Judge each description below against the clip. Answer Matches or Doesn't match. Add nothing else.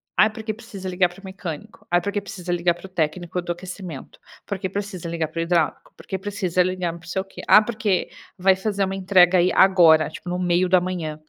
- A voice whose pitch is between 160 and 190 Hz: Matches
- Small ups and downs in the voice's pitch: Matches